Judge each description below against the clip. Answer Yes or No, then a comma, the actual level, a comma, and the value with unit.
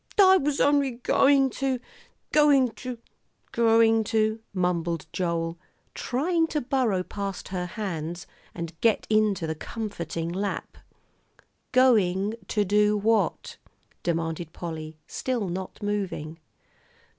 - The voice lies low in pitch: No, high, 210 Hz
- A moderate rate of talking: No, slow, 115 wpm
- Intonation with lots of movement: Yes, wide, 6.2 semitones